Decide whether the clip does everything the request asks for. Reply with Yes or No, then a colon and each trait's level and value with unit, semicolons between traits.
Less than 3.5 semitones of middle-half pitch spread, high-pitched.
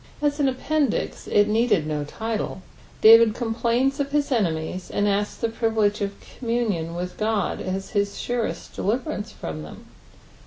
No: average, 3.9 semitones; high, 215 Hz